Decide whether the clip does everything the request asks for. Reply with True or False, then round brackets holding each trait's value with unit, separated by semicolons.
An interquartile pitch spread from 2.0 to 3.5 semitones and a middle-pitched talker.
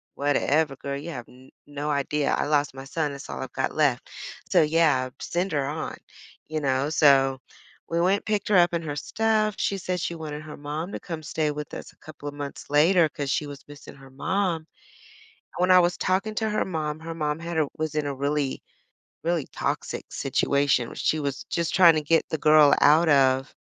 True (2.9 semitones; 150 Hz)